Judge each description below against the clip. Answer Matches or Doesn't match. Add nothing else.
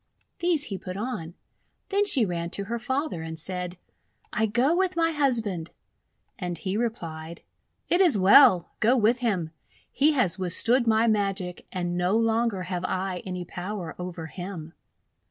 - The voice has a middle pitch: Doesn't match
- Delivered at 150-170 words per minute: Matches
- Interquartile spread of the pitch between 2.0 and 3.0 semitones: Doesn't match